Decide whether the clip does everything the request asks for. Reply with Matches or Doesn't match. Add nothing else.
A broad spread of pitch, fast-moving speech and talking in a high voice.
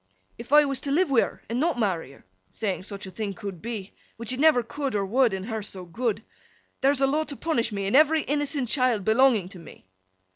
Matches